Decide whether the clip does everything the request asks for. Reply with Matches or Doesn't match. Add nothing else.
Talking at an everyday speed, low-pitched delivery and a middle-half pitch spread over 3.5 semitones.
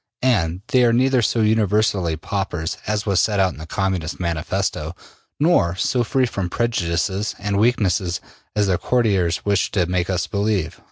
Matches